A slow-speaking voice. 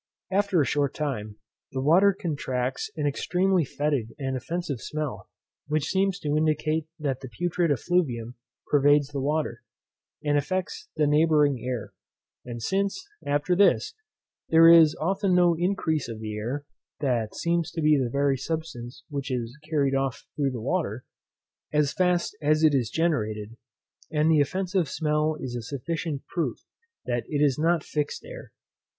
No: average, 155 wpm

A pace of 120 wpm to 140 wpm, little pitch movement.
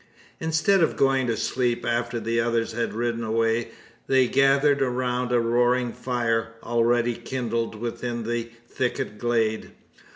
Yes: slow, 135 wpm; narrow, 1.5 semitones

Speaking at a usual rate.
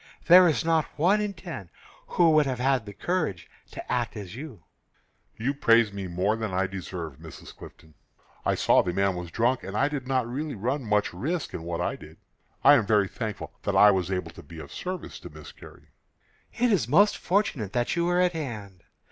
No: fast, 215 wpm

